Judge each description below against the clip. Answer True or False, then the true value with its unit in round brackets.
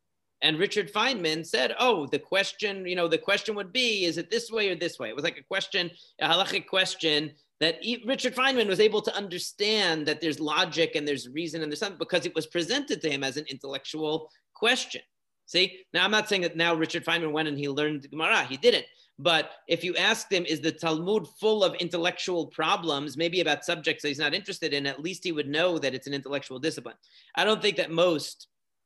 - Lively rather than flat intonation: False (4.4 semitones)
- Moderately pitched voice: True (170 Hz)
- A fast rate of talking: True (215 wpm)